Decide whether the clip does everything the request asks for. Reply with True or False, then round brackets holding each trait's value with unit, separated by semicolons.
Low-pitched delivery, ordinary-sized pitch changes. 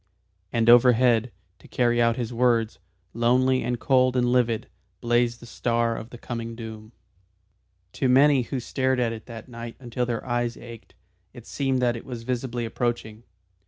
False (120 Hz; 1.4 semitones)